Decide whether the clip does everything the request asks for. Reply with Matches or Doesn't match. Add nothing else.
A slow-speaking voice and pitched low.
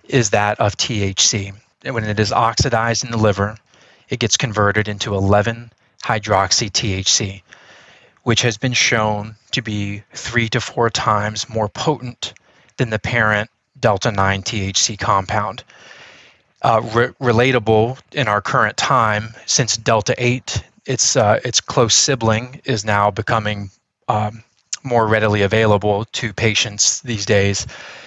Matches